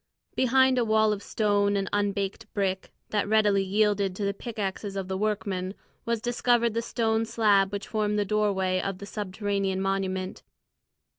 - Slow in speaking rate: No, average, 160 wpm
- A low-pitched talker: No, high, 205 Hz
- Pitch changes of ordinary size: No, narrow, 2.0 semitones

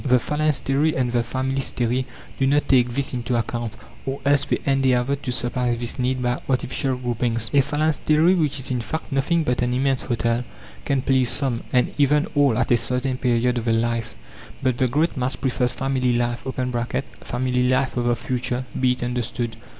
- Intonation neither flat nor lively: No, narrow, 2.0 semitones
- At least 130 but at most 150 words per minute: No, average, 185 wpm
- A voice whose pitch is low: Yes, low, 125 Hz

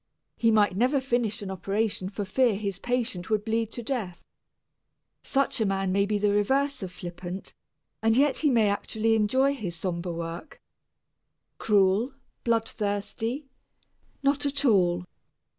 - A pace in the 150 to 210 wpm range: No, average, 140 wpm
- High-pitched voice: Yes, high, 215 Hz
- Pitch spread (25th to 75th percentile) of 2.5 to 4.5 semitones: Yes, average, 4.1 semitones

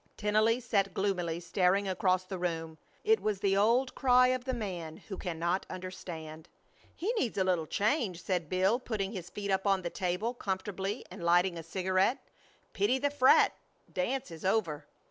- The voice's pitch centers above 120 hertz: Yes, high, 190 Hz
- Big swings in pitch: No, average, 3.9 semitones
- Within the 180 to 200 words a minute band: No, average, 170 wpm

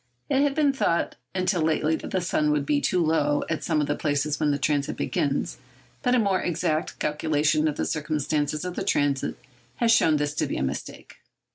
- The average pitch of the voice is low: No, medium, 155 Hz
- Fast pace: Yes, fast, 210 wpm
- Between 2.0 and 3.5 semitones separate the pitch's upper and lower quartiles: Yes, average, 3.1 semitones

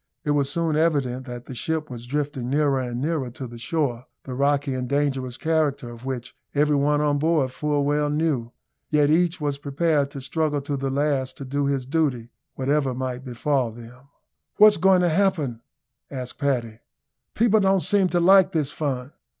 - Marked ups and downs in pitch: No, average, 3.1 semitones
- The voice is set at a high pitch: No, medium, 140 Hz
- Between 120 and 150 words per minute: No, average, 180 wpm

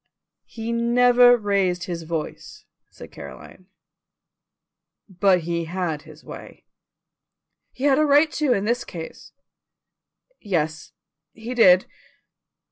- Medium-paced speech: No, slow, 110 wpm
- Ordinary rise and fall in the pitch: No, wide, 6.2 semitones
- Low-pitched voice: No, high, 195 Hz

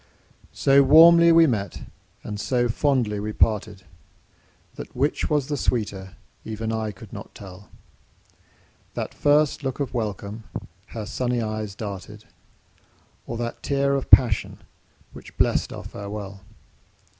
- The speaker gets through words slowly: Yes, slow, 130 wpm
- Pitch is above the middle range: No, low, 115 Hz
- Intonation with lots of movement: No, average, 4.9 semitones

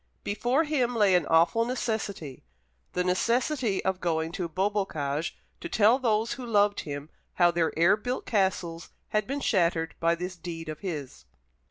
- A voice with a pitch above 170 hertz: Yes, high, 190 Hz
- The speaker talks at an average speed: Yes, average, 160 wpm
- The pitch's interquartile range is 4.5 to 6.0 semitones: Yes, average, 5.2 semitones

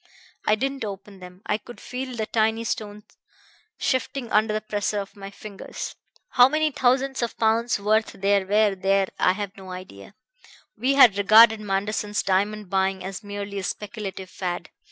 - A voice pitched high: Yes, high, 210 Hz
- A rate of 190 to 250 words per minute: No, average, 165 wpm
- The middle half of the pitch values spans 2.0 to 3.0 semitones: Yes, narrow, 2.5 semitones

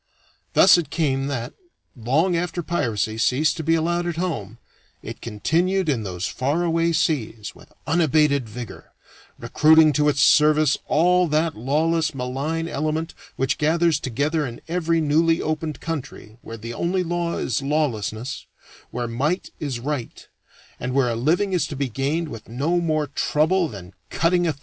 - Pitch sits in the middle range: Yes, medium, 150 Hz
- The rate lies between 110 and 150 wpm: No, average, 160 wpm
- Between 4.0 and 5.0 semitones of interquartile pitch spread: Yes, average, 4.5 semitones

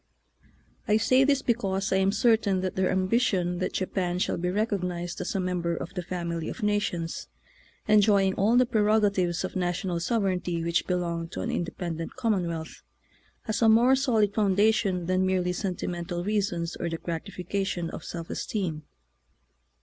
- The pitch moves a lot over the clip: No, average, 3.2 semitones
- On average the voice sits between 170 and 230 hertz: Yes, medium, 185 Hz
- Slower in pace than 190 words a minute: Yes, average, 160 wpm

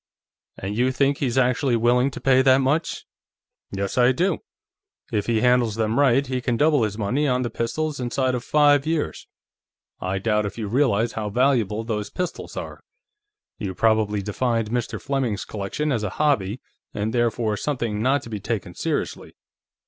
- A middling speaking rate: Yes, average, 170 wpm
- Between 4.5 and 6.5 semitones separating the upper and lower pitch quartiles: No, average, 3.9 semitones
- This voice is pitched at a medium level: No, low, 120 Hz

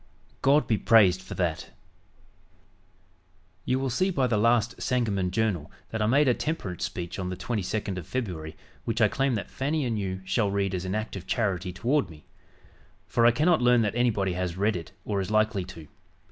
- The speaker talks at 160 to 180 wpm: No, average, 195 wpm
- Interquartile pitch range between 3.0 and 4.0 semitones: No, average, 4.6 semitones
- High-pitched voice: No, low, 105 Hz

